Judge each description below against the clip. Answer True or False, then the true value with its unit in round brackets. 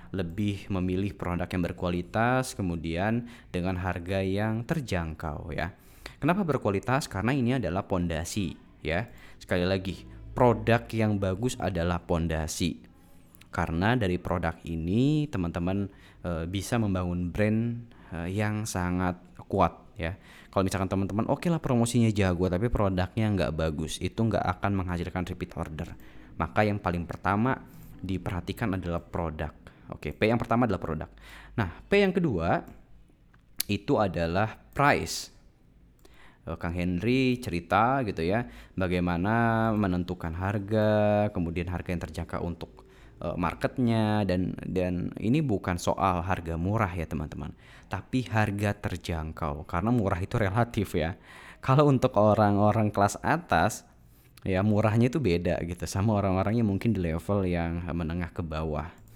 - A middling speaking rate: True (130 wpm)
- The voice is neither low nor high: False (95 Hz)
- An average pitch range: True (4.0 semitones)